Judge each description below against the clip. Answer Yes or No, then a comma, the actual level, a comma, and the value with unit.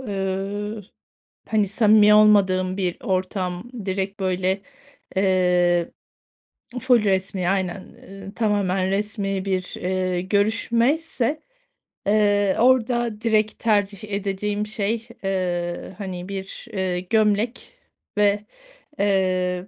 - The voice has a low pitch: No, high, 200 Hz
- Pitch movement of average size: No, narrow, 2.2 semitones